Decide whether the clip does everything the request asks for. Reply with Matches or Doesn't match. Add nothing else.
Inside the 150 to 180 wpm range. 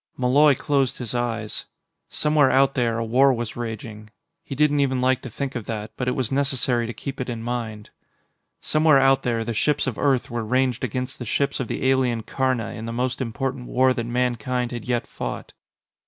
Doesn't match